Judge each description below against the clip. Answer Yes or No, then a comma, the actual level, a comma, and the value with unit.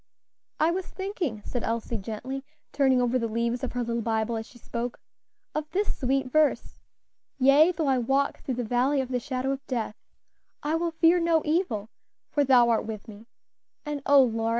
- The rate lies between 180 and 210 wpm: Yes, average, 190 wpm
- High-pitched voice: Yes, very high, 255 Hz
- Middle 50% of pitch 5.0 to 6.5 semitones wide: No, average, 4.1 semitones